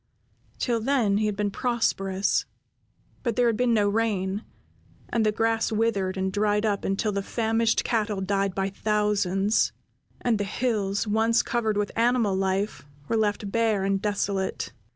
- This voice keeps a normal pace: Yes, average, 155 wpm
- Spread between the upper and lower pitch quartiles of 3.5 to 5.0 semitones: No, narrow, 2.4 semitones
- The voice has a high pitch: Yes, high, 210 Hz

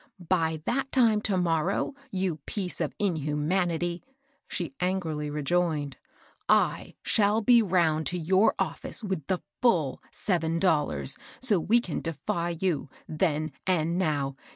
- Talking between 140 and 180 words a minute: Yes, average, 150 wpm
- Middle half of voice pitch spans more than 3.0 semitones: Yes, average, 3.7 semitones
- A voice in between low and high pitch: Yes, medium, 175 Hz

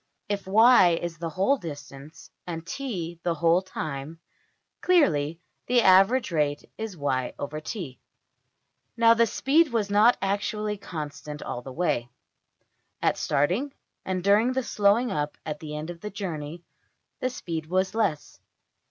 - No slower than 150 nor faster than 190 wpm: No, average, 140 wpm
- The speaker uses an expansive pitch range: Yes, wide, 5.9 semitones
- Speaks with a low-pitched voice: No, medium, 180 Hz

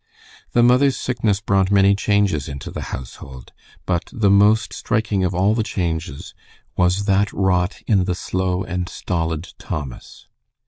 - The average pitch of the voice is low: Yes, very low, 95 Hz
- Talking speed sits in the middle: Yes, average, 145 wpm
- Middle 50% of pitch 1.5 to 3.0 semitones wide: Yes, average, 2.7 semitones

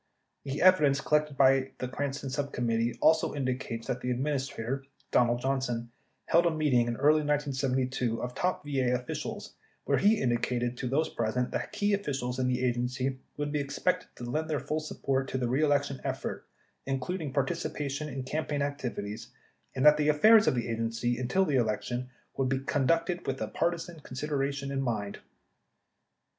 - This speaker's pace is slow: No, average, 165 wpm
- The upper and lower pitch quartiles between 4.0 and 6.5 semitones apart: No, average, 3.1 semitones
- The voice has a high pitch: No, low, 135 Hz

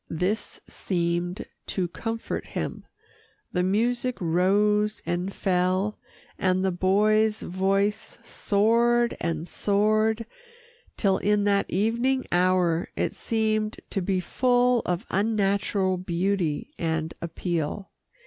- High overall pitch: Yes, high, 195 Hz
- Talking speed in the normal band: No, slow, 105 wpm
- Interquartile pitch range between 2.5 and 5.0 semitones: Yes, average, 3.1 semitones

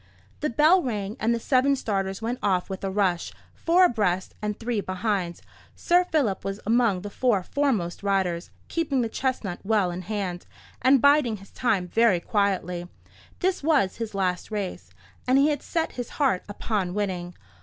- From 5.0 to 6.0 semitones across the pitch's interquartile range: Yes, average, 5.3 semitones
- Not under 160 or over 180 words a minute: Yes, average, 170 wpm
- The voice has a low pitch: No, high, 210 Hz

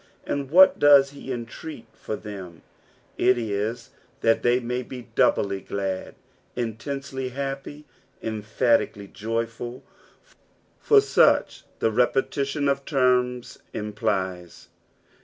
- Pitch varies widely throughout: No, average, 4.3 semitones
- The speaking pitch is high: No, low, 120 Hz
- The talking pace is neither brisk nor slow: No, slow, 100 wpm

